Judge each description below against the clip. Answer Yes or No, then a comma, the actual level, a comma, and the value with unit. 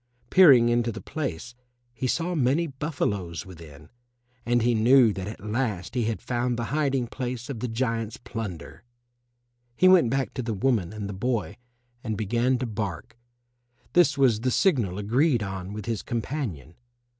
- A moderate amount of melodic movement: Yes, average, 4.1 semitones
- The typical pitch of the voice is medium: No, low, 115 Hz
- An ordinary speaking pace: Yes, average, 165 wpm